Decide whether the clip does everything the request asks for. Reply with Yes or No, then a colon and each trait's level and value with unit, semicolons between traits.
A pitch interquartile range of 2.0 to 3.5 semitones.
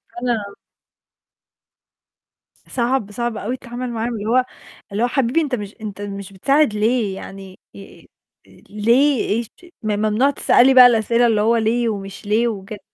Yes: average, 2.9 semitones